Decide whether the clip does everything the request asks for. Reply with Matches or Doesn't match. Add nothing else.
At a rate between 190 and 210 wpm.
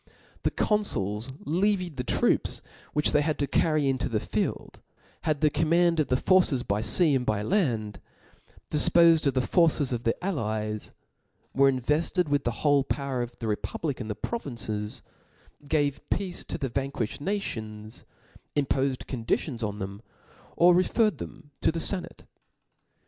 Doesn't match